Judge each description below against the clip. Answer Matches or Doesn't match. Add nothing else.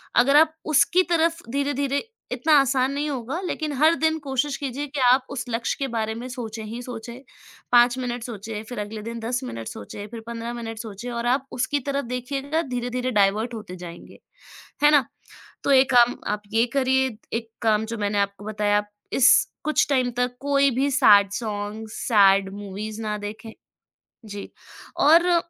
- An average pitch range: Matches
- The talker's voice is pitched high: Matches